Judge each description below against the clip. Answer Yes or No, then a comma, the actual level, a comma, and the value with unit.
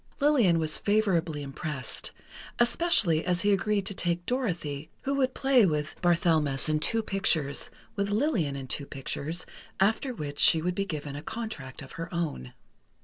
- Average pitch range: No, wide, 5.9 semitones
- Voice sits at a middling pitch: Yes, medium, 170 Hz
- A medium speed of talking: Yes, average, 160 wpm